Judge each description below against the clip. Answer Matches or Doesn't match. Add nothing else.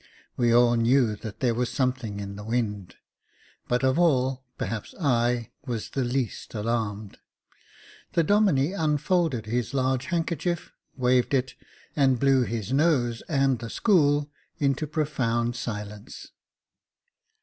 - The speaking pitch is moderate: Doesn't match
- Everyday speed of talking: Doesn't match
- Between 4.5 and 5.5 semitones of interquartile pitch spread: Doesn't match